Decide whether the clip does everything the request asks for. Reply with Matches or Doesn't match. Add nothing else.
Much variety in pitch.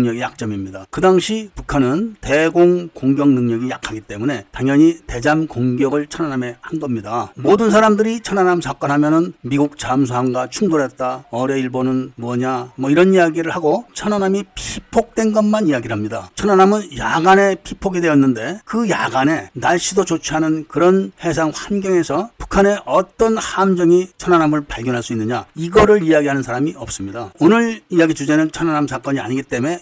Matches